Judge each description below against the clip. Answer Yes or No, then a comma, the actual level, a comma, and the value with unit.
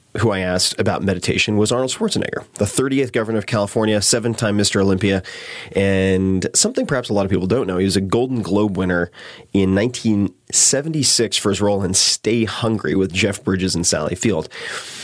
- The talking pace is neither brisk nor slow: Yes, average, 185 wpm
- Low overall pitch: Yes, low, 100 Hz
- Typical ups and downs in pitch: Yes, average, 3.1 semitones